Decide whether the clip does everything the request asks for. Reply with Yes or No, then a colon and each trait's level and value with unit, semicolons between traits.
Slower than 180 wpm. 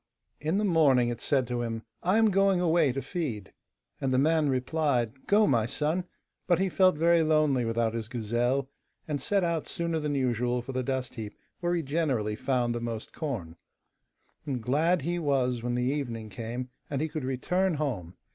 No: average, 185 wpm